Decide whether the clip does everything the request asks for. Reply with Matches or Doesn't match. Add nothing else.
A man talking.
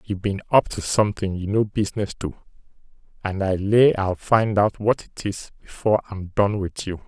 Matches